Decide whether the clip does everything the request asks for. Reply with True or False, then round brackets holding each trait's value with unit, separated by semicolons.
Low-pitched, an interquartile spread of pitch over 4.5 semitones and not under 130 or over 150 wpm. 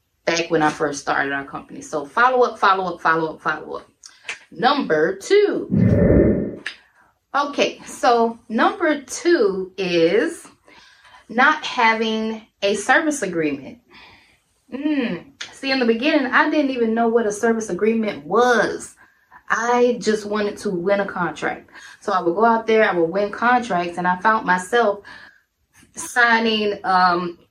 False (220 Hz; 5.5 semitones; 140 wpm)